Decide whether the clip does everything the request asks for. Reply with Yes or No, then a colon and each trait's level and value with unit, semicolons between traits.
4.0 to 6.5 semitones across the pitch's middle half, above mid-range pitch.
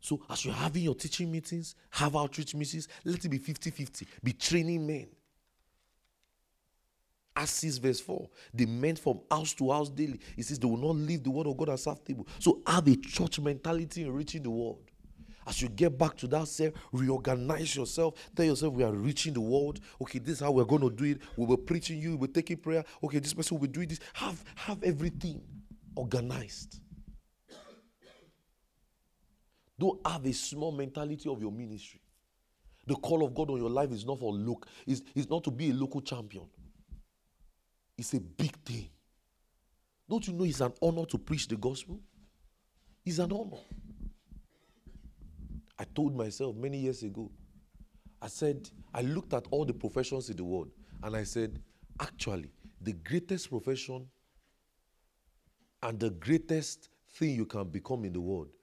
No: wide, 5.6 semitones; medium, 140 Hz